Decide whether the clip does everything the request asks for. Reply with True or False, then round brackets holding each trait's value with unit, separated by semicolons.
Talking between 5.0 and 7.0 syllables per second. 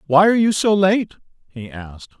True (5.7 syllables/s)